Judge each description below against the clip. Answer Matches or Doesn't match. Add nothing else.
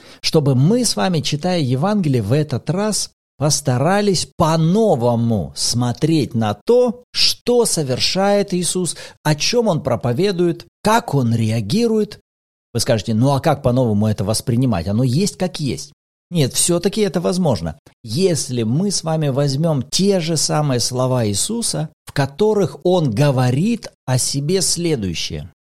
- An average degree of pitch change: Doesn't match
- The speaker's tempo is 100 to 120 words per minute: Doesn't match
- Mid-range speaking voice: Matches